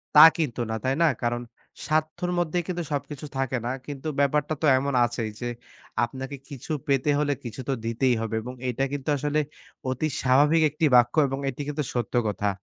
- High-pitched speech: No, low, 135 Hz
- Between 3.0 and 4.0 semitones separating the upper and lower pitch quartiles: Yes, average, 3.5 semitones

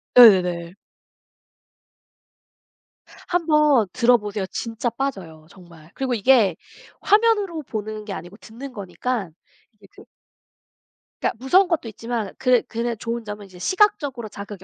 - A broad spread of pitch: No, average, 5.0 semitones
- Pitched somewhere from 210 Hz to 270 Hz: Yes, high, 225 Hz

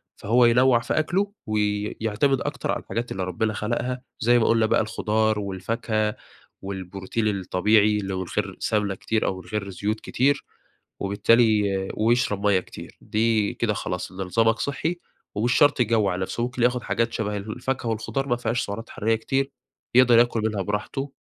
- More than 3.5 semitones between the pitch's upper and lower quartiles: No, average, 2.9 semitones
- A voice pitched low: Yes, low, 110 Hz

